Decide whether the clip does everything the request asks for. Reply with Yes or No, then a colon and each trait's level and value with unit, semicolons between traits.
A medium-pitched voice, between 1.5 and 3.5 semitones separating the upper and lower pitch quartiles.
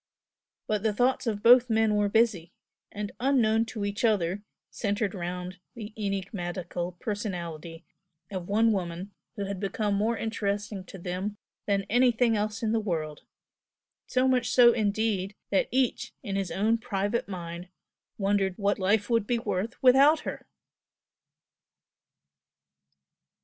No: high, 205 Hz; average, 3.1 semitones